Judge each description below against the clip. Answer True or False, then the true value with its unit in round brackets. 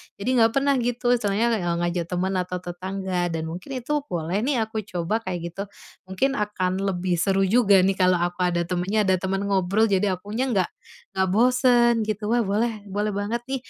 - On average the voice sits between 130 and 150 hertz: False (195 Hz)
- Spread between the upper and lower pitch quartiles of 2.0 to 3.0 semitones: False (3.6 semitones)